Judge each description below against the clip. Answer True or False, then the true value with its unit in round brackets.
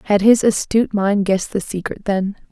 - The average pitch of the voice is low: False (205 Hz)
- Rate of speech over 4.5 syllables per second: True (5.4 syllables/s)